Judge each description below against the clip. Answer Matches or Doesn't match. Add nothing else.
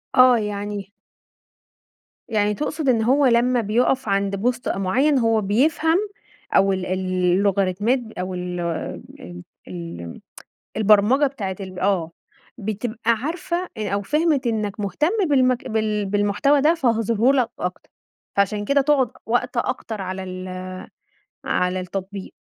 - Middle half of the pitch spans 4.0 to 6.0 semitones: Matches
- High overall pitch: Matches